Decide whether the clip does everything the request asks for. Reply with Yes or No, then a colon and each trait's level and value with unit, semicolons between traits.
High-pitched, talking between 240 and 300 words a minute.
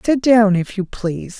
No: high, 205 Hz; fast, 215 wpm